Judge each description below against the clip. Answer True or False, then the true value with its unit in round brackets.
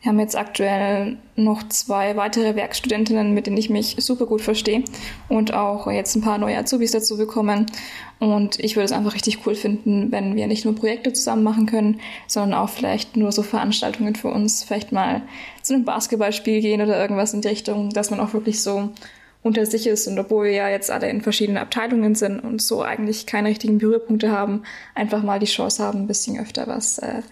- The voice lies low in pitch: False (215 Hz)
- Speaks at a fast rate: True (205 wpm)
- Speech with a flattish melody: True (1.4 semitones)